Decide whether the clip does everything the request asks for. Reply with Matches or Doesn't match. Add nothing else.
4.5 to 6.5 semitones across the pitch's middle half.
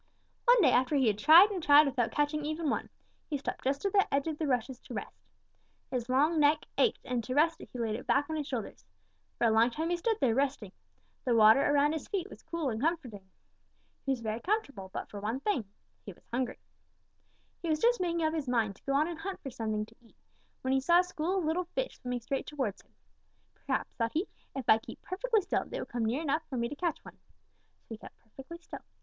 Matches